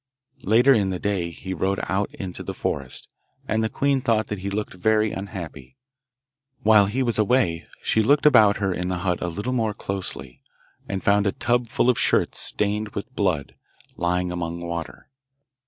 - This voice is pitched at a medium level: No, low, 100 Hz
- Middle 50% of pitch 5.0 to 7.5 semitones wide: No, average, 3.7 semitones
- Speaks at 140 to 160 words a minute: No, average, 180 wpm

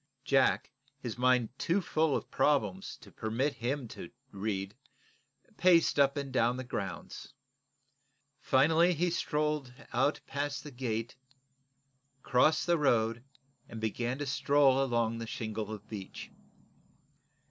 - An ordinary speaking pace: No, slow, 125 wpm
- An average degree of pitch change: Yes, average, 4.6 semitones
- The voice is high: No, low, 130 Hz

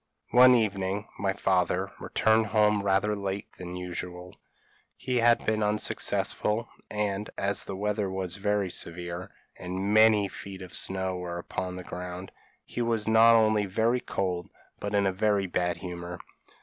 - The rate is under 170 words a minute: Yes, average, 155 wpm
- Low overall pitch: Yes, low, 100 Hz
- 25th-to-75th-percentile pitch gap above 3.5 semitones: No, narrow, 2.6 semitones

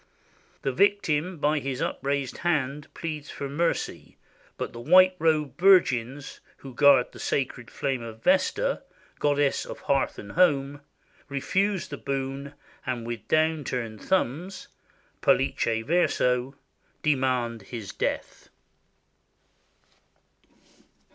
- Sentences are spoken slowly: Yes, slow, 115 wpm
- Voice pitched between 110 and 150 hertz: Yes, medium, 140 Hz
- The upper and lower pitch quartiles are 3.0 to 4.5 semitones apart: Yes, average, 4.2 semitones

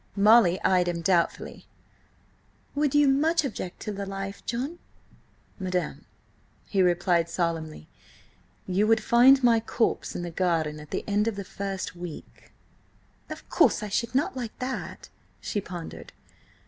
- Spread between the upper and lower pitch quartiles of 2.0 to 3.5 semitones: No, average, 5.2 semitones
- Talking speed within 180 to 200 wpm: No, average, 145 wpm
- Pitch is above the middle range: Yes, high, 195 Hz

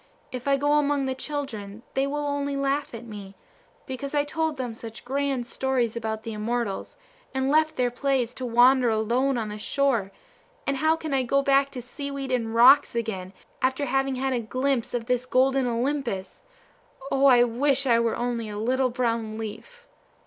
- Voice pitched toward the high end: Yes, very high, 255 Hz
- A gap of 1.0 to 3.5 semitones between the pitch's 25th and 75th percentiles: Yes, average, 3.1 semitones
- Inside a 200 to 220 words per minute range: No, average, 185 wpm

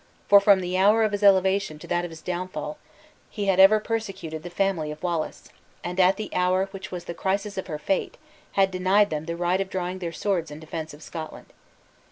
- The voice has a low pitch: No, medium, 185 Hz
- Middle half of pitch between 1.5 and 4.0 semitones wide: Yes, narrow, 2.5 semitones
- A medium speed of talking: No, fast, 220 wpm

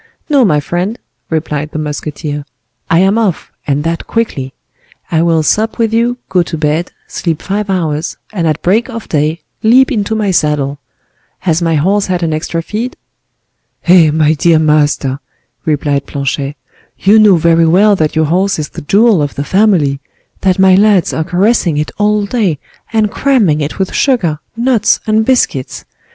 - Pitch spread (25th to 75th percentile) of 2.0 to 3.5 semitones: No, wide, 5.6 semitones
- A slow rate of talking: No, average, 170 wpm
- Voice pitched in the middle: Yes, medium, 170 Hz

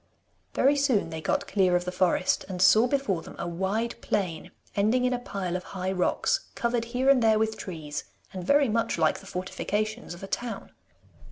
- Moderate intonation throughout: Yes, average, 5.0 semitones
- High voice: Yes, high, 205 Hz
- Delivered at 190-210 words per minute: Yes, average, 195 wpm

